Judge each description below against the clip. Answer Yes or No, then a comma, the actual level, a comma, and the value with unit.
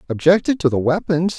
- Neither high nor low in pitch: Yes, medium, 165 Hz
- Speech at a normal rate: Yes, average, 175 wpm